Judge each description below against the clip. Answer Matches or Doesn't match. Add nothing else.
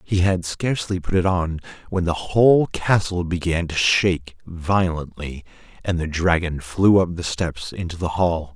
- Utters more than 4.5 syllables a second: Doesn't match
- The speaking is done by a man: Matches